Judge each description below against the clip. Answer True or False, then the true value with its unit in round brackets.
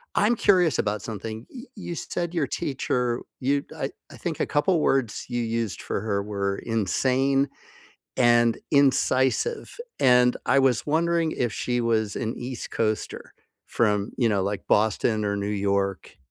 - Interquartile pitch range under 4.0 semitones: False (4.5 semitones)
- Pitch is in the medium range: False (120 Hz)